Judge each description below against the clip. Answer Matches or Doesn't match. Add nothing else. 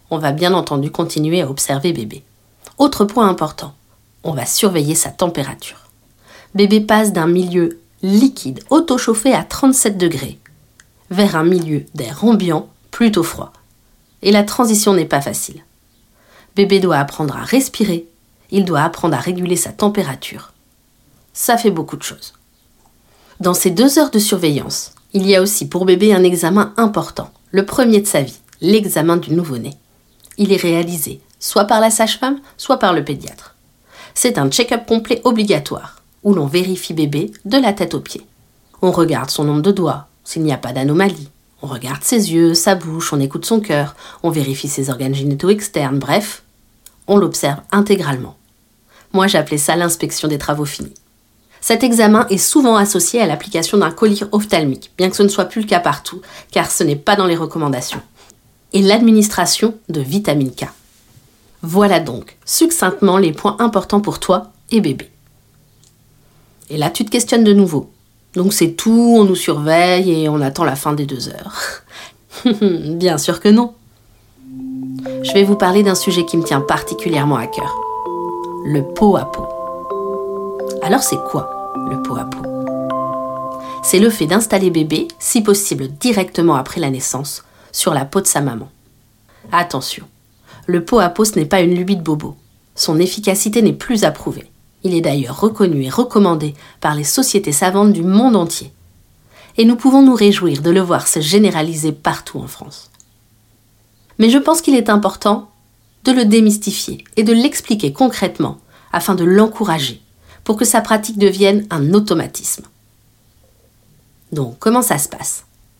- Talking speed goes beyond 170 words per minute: Doesn't match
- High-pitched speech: Doesn't match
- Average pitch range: Doesn't match